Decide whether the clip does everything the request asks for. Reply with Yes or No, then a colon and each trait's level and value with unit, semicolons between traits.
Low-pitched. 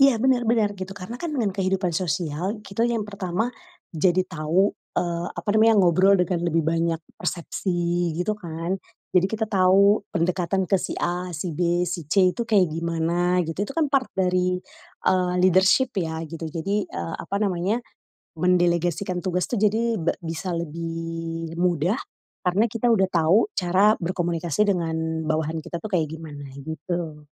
No: medium, 180 Hz